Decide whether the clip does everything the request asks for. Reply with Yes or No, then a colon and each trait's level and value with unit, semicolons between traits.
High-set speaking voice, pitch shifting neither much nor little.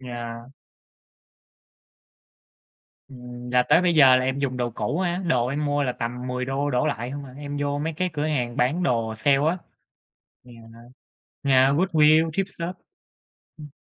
No: low, 135 Hz; average, 3.5 semitones